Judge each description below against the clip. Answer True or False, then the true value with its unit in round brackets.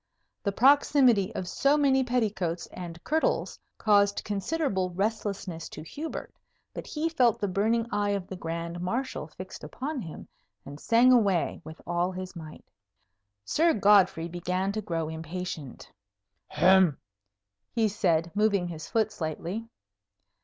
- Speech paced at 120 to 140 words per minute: True (135 wpm)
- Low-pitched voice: False (195 Hz)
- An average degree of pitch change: True (4.8 semitones)